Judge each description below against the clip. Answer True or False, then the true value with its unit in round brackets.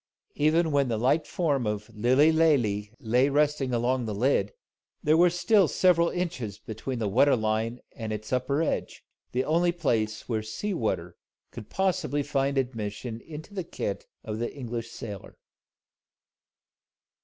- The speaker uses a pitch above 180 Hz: False (130 Hz)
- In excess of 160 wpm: False (150 wpm)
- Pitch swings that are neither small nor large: False (6.0 semitones)